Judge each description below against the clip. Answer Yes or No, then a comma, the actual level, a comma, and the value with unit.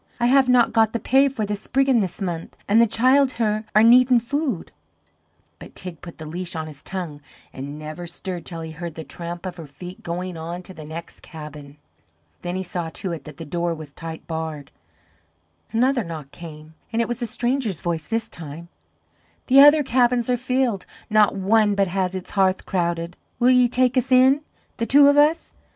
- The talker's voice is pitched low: No, high, 190 Hz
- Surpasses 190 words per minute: Yes, average, 200 wpm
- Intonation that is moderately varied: No, wide, 6.6 semitones